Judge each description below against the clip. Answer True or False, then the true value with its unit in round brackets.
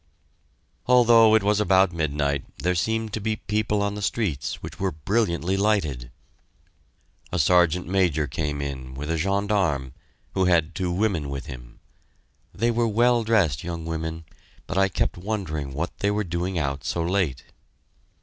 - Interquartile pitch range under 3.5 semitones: False (5.3 semitones)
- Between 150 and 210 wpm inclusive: True (160 wpm)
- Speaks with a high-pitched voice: False (90 Hz)